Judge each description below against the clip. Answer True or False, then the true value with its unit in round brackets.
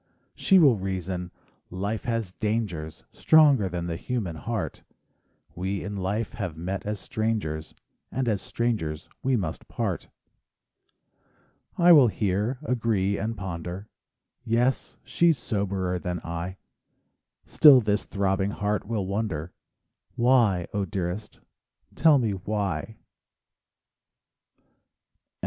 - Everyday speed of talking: False (110 wpm)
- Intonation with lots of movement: False (3.9 semitones)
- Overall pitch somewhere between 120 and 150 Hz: False (100 Hz)